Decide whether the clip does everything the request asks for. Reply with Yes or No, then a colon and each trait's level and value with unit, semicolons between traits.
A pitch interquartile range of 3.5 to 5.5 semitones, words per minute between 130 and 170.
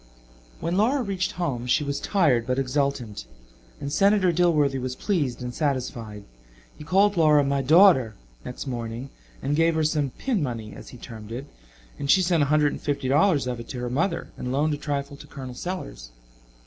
No: average, 5.0 semitones; average, 190 wpm